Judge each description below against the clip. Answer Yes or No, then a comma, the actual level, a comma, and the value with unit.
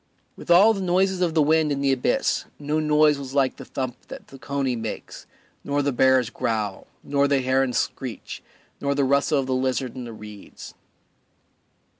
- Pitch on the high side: No, medium, 140 Hz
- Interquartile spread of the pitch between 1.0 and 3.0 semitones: Yes, average, 2.7 semitones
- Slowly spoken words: No, average, 185 wpm